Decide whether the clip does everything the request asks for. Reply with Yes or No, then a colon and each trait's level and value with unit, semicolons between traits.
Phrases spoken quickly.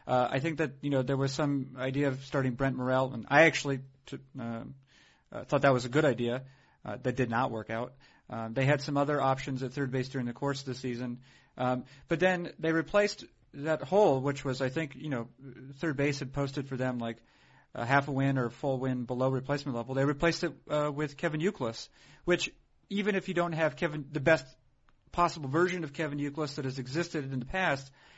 Yes: fast, 225 wpm